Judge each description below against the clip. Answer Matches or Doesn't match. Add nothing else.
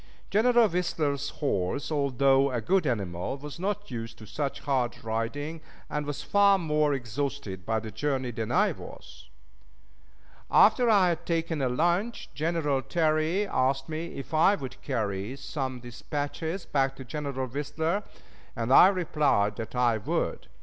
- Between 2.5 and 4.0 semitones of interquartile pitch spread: Doesn't match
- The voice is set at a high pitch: Doesn't match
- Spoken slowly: Doesn't match